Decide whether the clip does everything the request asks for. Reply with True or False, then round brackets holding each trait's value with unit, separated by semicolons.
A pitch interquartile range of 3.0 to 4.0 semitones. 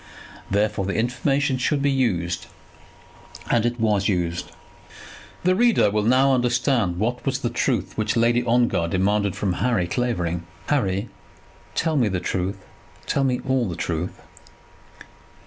False (5.1 semitones)